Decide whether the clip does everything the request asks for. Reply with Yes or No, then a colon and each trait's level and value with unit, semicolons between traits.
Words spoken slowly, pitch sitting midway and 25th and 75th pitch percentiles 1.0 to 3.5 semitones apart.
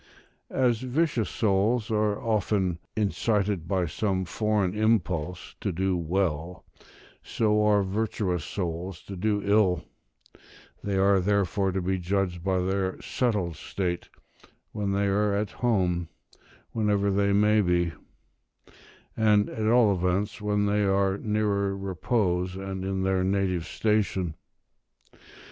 No: slow, 125 wpm; low, 100 Hz; narrow, 2.4 semitones